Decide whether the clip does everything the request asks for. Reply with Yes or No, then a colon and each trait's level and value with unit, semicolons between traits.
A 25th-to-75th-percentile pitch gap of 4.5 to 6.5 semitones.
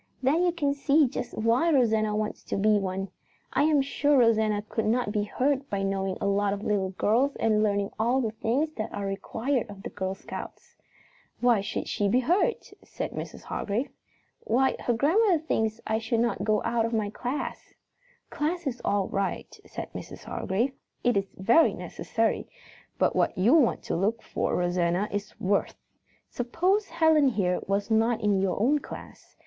Yes: average, 5.1 semitones